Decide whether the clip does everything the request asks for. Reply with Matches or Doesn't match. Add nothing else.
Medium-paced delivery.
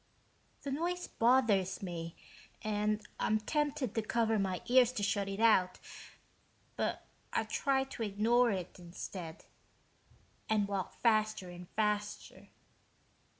Doesn't match